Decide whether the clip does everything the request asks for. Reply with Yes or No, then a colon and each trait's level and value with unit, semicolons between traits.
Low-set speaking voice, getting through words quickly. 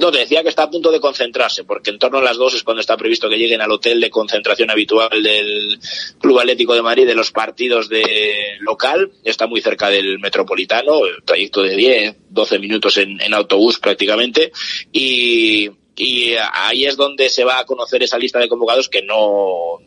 Yes: low, 125 Hz; fast, 195 wpm